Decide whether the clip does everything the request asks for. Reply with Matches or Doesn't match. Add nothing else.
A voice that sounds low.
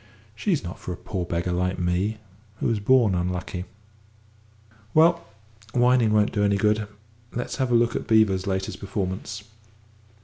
Matches